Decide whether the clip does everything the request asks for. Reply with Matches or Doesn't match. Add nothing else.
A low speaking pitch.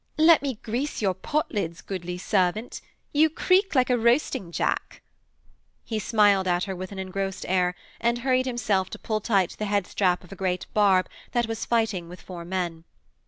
Doesn't match